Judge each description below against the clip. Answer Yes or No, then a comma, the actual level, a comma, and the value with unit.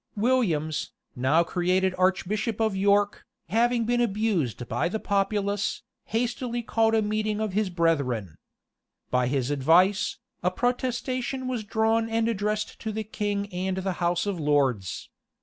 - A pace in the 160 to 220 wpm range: No, average, 145 wpm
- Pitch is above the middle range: Yes, high, 200 Hz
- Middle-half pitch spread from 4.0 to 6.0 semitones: Yes, average, 4.5 semitones